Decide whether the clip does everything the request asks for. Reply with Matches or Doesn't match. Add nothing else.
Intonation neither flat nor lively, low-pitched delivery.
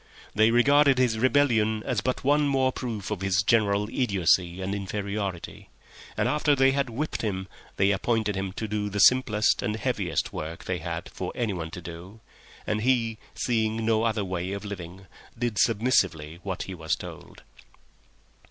Matches